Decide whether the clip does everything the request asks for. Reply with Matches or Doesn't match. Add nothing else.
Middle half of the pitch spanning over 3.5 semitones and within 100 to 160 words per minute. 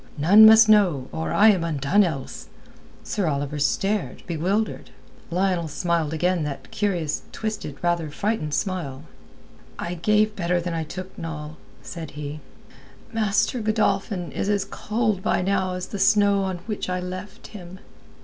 Matches